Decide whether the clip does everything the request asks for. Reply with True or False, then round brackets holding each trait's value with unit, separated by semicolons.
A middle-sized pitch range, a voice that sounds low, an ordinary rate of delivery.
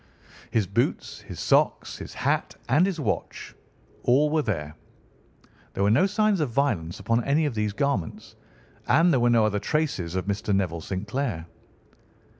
False (7.2 semitones; 115 Hz; 160 wpm)